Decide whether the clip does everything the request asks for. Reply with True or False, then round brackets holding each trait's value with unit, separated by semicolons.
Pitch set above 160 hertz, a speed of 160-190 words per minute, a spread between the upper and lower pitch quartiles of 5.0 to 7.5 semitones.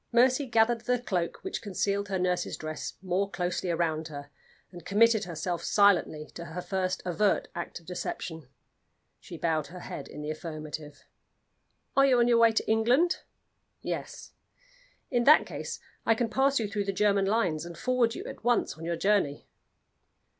True (190 Hz; 170 wpm; 5.3 semitones)